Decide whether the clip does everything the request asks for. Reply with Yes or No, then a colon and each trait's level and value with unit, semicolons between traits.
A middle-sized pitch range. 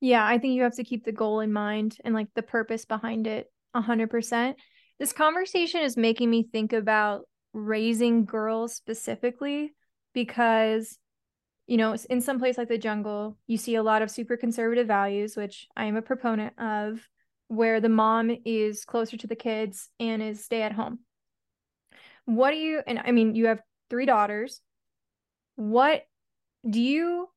No: narrow, 2.0 semitones